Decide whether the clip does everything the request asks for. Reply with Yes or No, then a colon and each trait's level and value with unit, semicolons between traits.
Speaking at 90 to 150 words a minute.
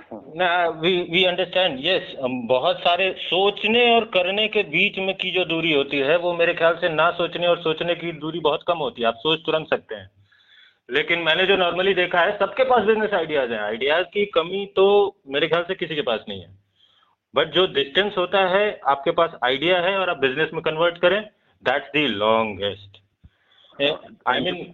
No: fast, 190 wpm